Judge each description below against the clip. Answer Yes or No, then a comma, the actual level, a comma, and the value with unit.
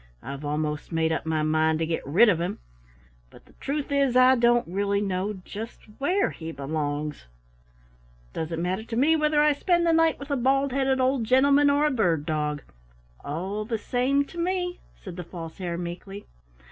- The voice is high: Yes, high, 210 Hz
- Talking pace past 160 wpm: Yes, average, 185 wpm